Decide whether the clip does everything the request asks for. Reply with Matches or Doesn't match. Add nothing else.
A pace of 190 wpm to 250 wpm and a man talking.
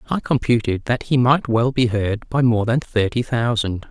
Matches